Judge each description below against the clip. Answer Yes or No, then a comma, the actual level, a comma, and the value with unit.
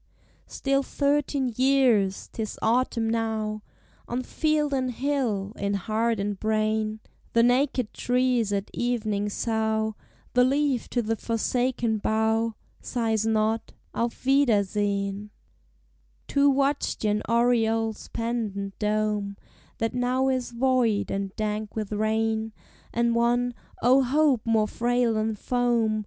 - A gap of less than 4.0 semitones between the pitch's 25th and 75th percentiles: Yes, narrow, 2.5 semitones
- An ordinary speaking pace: No, slow, 120 wpm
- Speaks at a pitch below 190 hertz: No, high, 225 Hz